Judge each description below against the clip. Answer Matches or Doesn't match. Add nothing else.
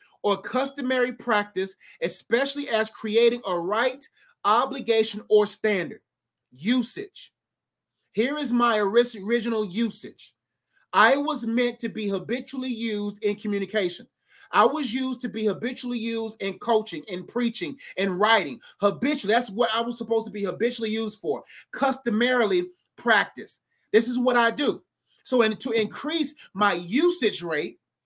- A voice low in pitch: Doesn't match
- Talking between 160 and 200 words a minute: Doesn't match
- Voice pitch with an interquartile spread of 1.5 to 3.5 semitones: Matches